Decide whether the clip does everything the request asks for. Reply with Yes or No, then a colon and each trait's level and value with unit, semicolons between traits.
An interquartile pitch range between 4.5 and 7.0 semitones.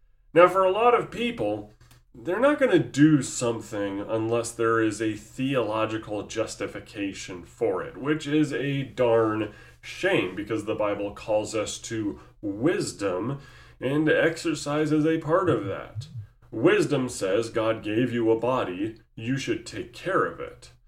Yes: wide, 5.6 semitones